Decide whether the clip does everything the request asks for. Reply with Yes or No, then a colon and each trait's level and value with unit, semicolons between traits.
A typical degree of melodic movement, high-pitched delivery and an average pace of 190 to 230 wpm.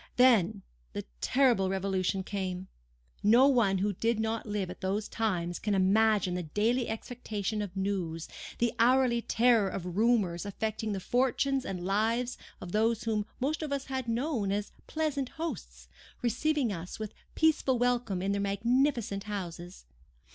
No: average, 4.2 semitones; high, 215 Hz; average, 145 wpm